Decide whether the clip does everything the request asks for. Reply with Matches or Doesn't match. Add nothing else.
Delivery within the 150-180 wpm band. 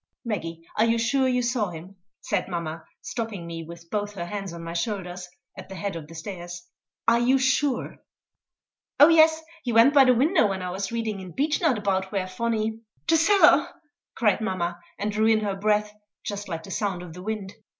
Doesn't match